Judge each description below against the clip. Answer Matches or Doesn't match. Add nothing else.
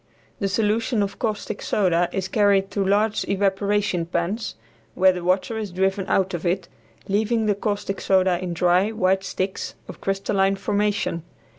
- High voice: Matches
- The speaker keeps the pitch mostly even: Matches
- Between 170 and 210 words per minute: Doesn't match